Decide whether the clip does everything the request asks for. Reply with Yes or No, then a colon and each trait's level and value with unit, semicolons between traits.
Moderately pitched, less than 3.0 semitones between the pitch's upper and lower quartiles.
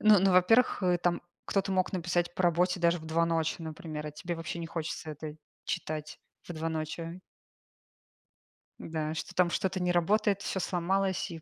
Yes: medium, 175 Hz; narrow, 2.5 semitones